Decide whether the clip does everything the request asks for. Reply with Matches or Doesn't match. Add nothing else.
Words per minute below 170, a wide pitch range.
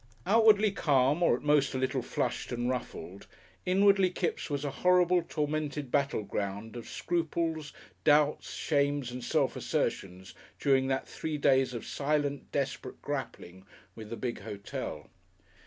Doesn't match